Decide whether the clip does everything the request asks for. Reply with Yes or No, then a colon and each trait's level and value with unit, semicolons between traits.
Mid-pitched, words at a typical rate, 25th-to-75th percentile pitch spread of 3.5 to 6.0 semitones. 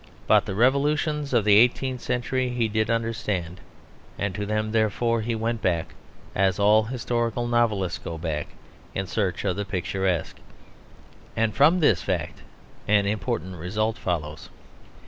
No: low, 110 Hz; average, 145 wpm; average, 3.8 semitones